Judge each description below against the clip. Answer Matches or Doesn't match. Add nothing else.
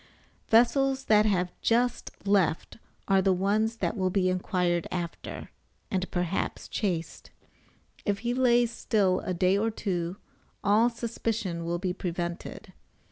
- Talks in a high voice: Matches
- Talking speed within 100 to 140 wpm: Matches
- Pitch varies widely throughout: Doesn't match